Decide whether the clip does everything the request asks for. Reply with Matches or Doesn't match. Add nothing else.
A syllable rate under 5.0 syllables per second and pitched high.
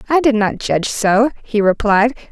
Matches